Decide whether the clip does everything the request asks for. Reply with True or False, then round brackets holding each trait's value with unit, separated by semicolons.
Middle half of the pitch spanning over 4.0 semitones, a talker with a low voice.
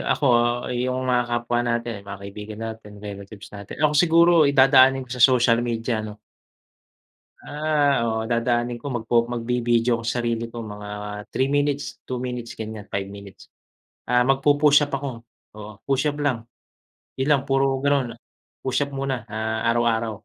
False (3.3 semitones; 120 Hz)